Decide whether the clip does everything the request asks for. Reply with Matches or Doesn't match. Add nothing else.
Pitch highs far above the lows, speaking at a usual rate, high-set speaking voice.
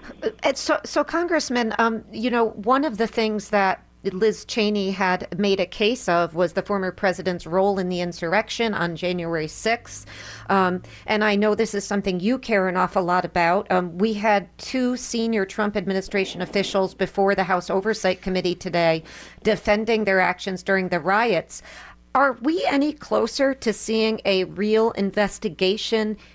Doesn't match